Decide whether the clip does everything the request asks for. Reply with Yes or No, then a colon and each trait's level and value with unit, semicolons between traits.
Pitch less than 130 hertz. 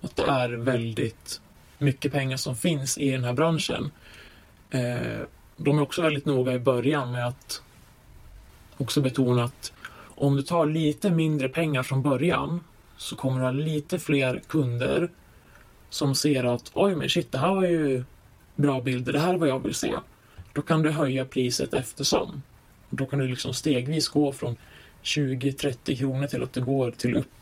No: low, 135 Hz